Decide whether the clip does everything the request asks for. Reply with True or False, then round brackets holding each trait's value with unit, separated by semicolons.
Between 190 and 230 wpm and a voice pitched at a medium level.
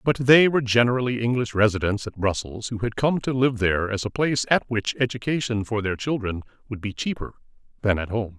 False (205 wpm; 115 Hz)